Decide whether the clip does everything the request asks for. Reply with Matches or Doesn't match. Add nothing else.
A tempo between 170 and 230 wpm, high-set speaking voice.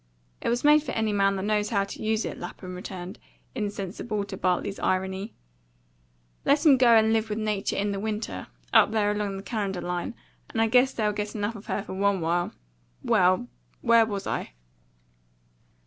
Matches